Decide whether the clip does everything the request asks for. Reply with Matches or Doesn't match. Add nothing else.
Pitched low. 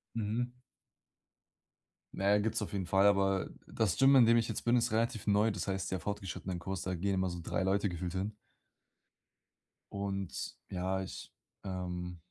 Matches